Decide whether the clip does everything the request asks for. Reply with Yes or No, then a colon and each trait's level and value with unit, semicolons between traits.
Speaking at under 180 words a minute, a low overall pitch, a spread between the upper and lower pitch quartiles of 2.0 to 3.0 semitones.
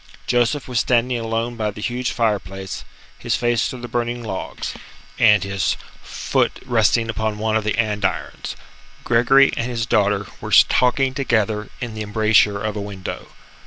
Yes: average, 160 wpm; low, 115 Hz; narrow, 2.4 semitones